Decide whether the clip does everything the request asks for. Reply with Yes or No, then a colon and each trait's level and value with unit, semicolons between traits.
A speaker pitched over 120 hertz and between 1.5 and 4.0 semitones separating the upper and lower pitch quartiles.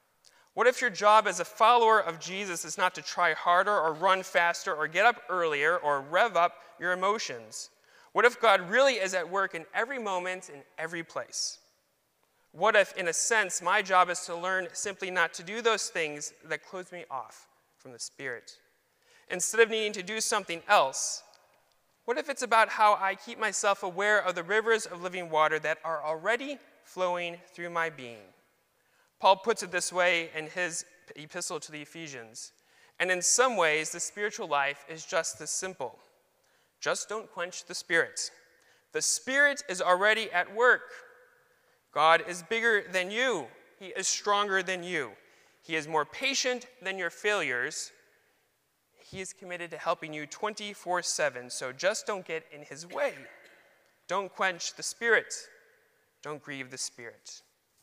No: medium, 185 Hz; average, 4.4 semitones